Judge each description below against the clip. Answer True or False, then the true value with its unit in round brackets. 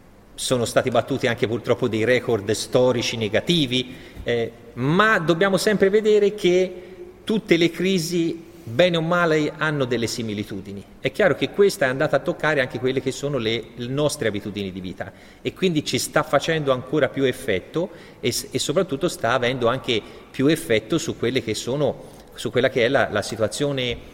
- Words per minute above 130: True (165 wpm)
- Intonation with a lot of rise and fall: True (6.4 semitones)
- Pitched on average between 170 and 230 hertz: False (135 Hz)